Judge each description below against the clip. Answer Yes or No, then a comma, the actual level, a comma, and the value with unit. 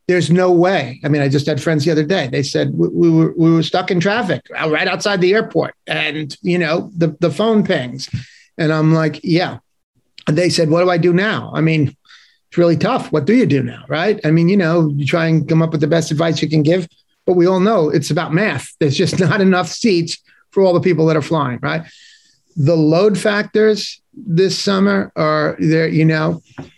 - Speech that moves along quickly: Yes, fast, 225 wpm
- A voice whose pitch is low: No, medium, 165 Hz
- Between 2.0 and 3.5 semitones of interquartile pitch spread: Yes, average, 2.9 semitones